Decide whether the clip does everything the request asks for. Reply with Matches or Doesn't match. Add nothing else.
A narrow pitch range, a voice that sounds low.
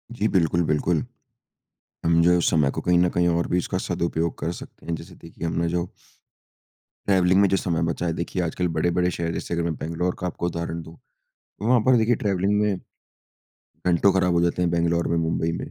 Matches